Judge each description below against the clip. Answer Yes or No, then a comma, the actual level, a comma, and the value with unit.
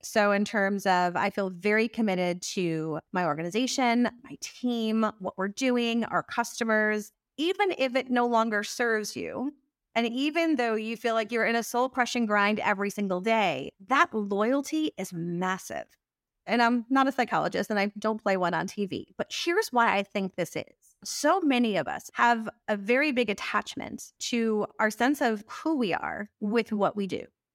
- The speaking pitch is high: Yes, high, 225 Hz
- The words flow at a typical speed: Yes, average, 180 wpm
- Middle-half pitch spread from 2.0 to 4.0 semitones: Yes, average, 3.3 semitones